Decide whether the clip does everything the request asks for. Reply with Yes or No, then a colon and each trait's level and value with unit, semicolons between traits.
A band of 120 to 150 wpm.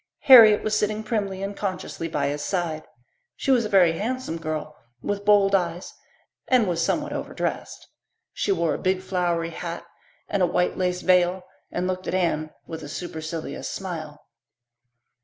No: average, 160 wpm